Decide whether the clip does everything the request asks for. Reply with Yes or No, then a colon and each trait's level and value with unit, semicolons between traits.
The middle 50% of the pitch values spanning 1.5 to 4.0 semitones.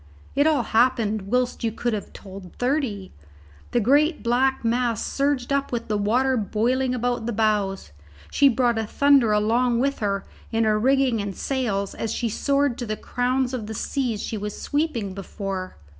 Yes: average, 3.7 semitones